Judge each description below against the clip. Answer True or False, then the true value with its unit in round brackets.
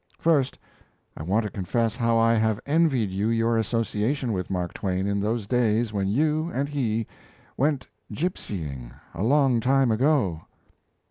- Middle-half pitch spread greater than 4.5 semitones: True (4.9 semitones)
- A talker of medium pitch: False (115 Hz)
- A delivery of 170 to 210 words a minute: False (150 wpm)